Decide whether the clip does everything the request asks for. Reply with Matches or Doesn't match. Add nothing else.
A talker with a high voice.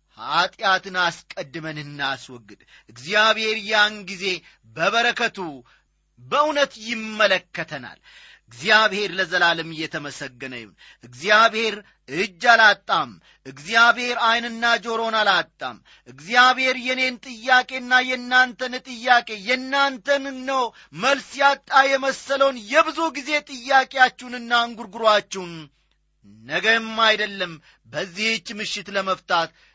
Matches